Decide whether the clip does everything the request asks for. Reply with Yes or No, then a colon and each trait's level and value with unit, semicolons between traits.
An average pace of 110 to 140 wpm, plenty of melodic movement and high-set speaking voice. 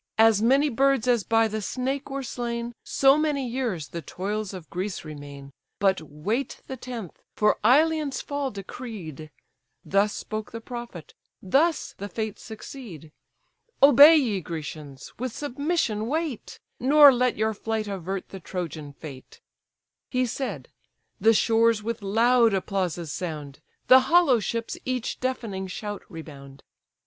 Yes: slow, 135 wpm; wide, 5.7 semitones; high, 220 Hz